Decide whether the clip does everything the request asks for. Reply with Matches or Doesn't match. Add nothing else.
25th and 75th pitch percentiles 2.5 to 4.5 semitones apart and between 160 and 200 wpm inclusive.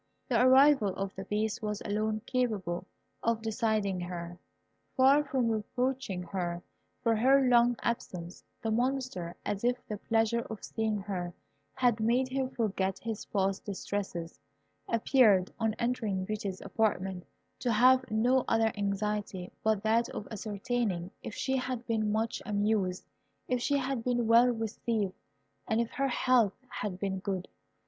Doesn't match